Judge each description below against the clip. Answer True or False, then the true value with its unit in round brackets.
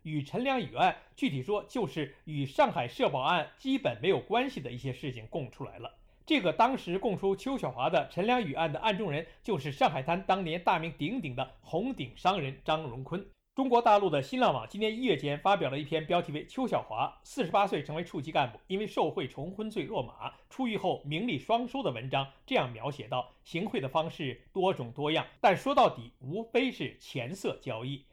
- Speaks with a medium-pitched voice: True (165 Hz)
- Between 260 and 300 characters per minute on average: False (310 characters per minute)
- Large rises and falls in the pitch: True (7.4 semitones)